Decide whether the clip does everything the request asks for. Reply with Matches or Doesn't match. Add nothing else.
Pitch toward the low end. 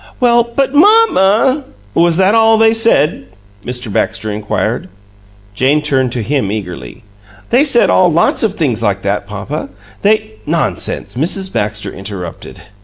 Doesn't match